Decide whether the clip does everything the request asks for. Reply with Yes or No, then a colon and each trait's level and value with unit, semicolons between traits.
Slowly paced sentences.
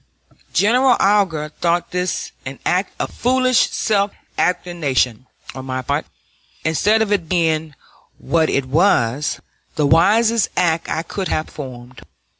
Yes: slow, 130 wpm